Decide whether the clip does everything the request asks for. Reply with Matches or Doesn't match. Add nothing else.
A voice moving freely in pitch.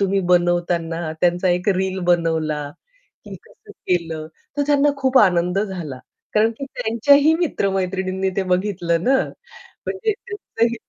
Matches